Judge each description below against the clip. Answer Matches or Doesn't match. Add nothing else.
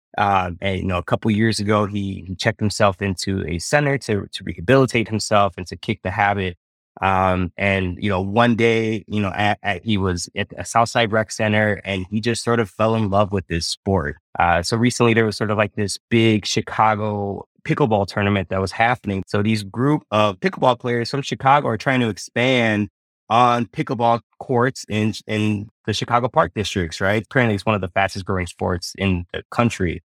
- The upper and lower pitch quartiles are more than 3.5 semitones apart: Doesn't match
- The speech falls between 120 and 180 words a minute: Doesn't match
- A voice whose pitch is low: Matches